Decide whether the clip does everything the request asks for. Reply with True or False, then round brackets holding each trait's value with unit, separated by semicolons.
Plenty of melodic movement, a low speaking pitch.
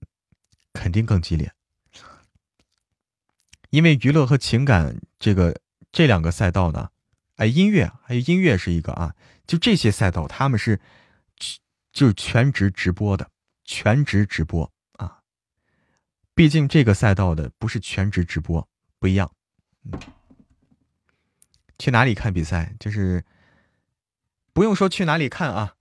True (7.0 semitones; 105 Hz)